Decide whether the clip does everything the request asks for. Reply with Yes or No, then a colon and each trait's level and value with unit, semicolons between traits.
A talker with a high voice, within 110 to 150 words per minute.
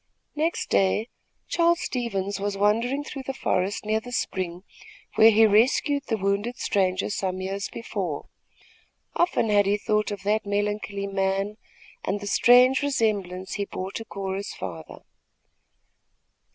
Yes: high, 205 Hz; average, 140 wpm